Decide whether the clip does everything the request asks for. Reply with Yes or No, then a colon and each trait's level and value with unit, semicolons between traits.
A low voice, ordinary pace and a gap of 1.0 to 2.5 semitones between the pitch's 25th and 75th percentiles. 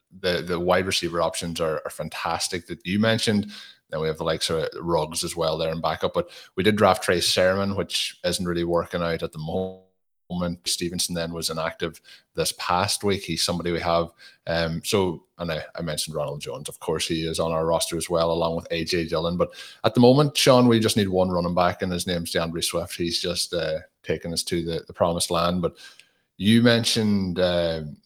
No: very low, 85 Hz; fast, 210 wpm; narrow, 2.1 semitones